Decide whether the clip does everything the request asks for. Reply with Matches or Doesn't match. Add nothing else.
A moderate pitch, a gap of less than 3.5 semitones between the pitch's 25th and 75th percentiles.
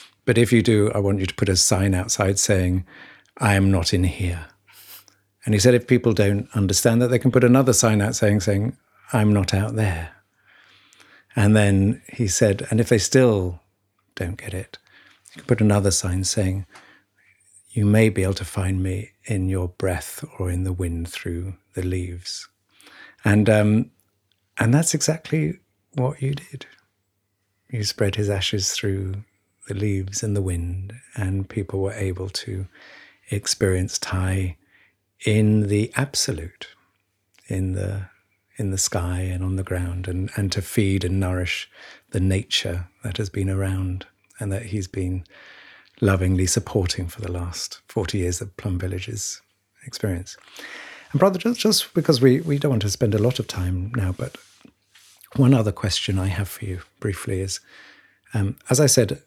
Doesn't match